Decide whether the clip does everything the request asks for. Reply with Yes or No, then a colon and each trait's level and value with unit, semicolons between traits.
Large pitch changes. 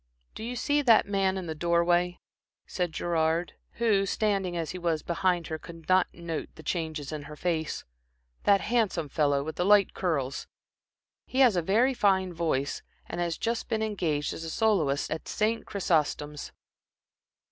No: average, 4.0 semitones